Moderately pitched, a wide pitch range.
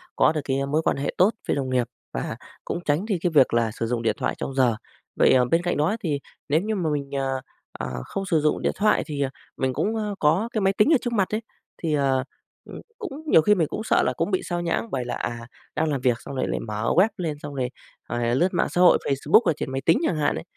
Yes: medium, 150 Hz; wide, 5.9 semitones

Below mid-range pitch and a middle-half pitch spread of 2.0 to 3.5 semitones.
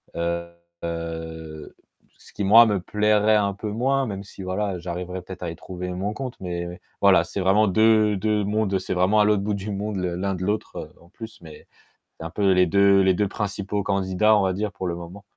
Yes: low, 100 Hz; narrow, 2.5 semitones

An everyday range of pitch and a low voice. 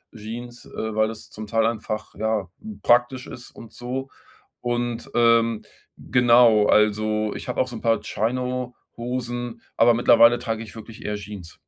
No: narrow, 2.0 semitones; low, 115 Hz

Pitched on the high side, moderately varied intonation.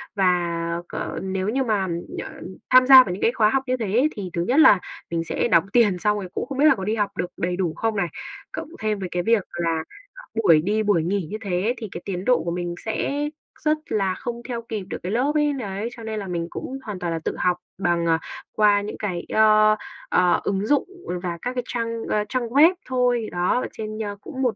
Yes: high, 210 Hz; average, 4.9 semitones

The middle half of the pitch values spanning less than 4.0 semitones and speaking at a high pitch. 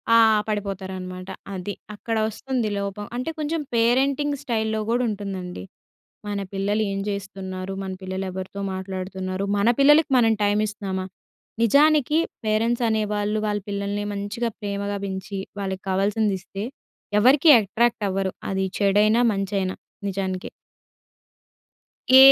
Yes: average, 2.8 semitones; high, 205 Hz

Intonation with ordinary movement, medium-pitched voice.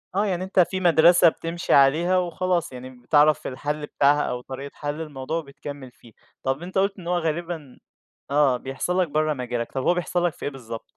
Yes: average, 4.5 semitones; medium, 150 Hz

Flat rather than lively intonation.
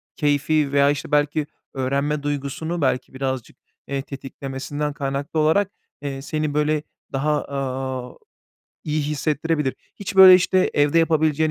Yes: narrow, 2.1 semitones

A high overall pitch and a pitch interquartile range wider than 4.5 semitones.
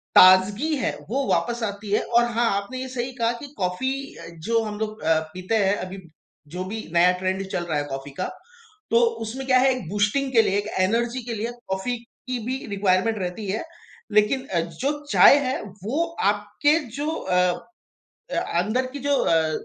Yes: high, 215 Hz; average, 5.2 semitones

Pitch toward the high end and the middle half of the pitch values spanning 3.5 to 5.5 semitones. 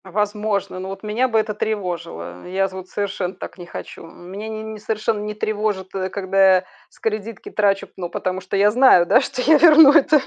No: high, 205 Hz; narrow, 2.6 semitones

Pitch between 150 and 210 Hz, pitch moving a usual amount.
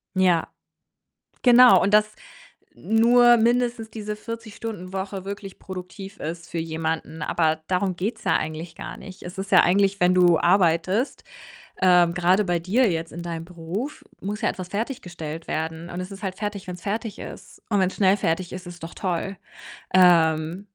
Yes: medium, 185 Hz; average, 3.4 semitones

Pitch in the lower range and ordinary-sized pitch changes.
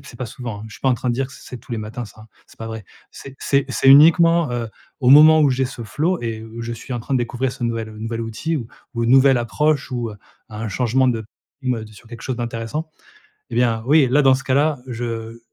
Yes: low, 120 Hz; average, 3.0 semitones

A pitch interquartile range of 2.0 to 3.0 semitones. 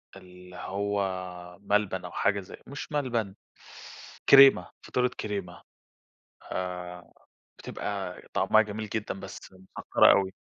Yes: average, 2.7 semitones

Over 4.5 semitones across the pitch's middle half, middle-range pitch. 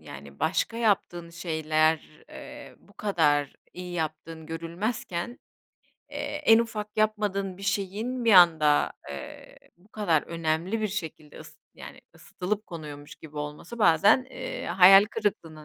Yes: average, 4.9 semitones; medium, 175 Hz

